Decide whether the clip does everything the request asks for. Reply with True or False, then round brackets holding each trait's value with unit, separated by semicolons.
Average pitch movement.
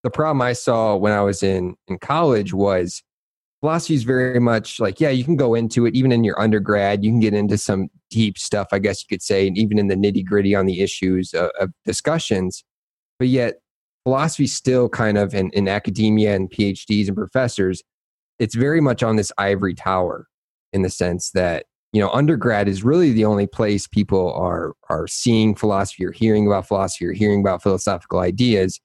True (3.6 semitones)